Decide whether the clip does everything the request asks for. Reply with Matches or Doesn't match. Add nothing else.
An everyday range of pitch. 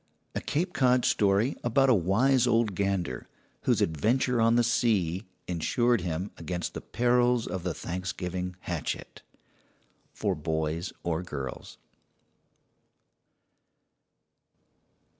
Doesn't match